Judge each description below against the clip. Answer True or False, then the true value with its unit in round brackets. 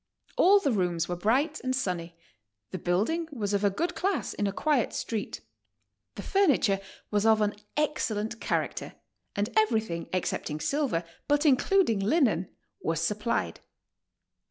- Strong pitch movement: True (7.4 semitones)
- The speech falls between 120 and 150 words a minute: True (145 wpm)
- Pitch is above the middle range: True (220 Hz)